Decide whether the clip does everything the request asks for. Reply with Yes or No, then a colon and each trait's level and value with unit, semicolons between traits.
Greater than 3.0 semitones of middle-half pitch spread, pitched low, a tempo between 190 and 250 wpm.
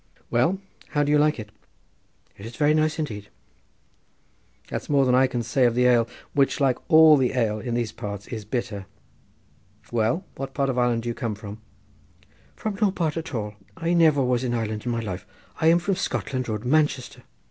Yes: average, 4.7 semitones; low, 125 Hz; average, 195 wpm